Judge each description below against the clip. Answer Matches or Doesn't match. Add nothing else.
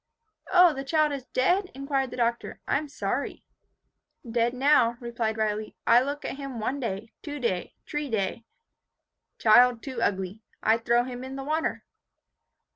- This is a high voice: Matches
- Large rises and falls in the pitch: Doesn't match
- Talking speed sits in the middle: Matches